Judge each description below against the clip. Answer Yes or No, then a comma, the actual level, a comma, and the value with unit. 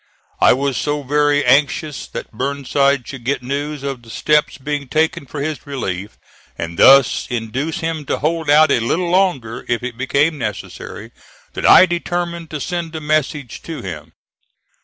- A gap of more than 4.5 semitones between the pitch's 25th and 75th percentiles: No, average, 3.7 semitones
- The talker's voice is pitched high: No, medium, 140 Hz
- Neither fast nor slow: Yes, average, 165 wpm